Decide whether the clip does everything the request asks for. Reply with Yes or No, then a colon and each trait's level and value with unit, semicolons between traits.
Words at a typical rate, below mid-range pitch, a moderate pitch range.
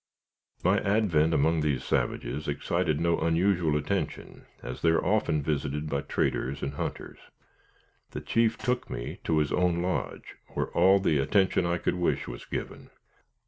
Yes: average, 155 wpm; very low, 80 Hz; average, 3.8 semitones